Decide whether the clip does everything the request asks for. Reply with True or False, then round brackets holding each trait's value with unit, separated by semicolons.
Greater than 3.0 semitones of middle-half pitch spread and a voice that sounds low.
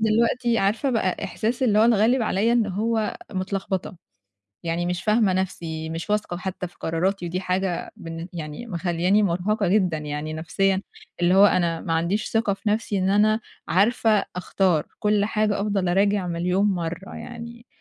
False (3.5 semitones; 195 Hz)